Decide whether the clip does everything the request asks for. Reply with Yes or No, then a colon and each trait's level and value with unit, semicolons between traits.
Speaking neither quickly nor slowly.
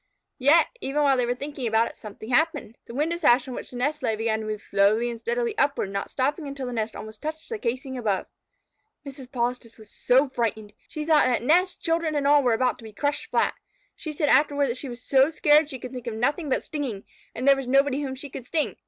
No: fast, 245 wpm